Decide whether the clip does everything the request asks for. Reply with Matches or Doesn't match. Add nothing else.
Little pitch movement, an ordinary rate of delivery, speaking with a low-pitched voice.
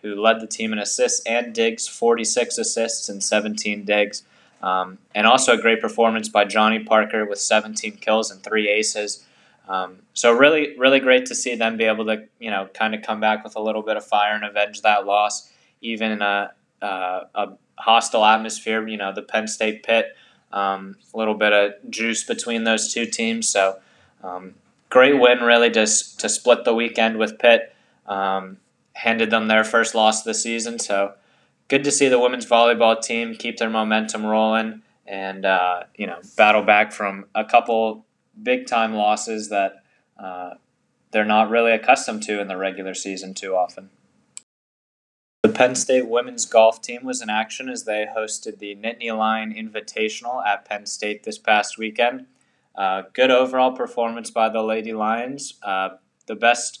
Matches